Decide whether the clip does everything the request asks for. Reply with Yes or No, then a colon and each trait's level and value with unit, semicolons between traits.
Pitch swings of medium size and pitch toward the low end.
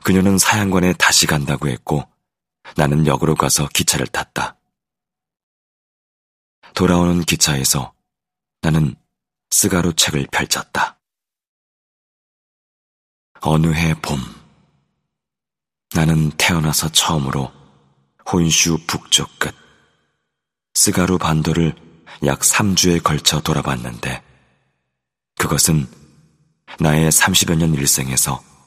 Yes: average, 3.6 semitones; very low, 80 Hz